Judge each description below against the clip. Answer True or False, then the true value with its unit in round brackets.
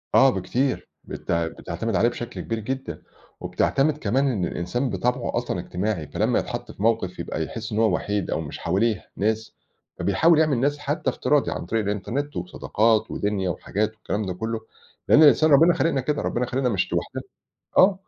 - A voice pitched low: True (115 Hz)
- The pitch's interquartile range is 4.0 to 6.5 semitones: True (5.2 semitones)